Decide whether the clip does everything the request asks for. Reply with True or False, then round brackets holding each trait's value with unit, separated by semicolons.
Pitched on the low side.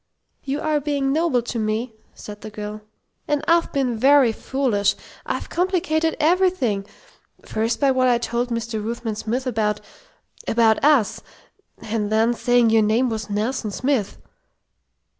False (240 Hz)